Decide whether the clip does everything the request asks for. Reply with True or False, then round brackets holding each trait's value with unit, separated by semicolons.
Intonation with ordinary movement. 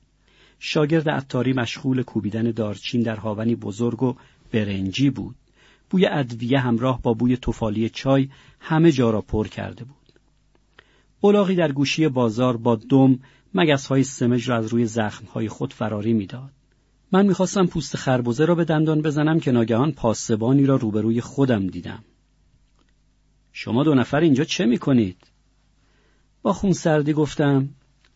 True (4.3 semitones)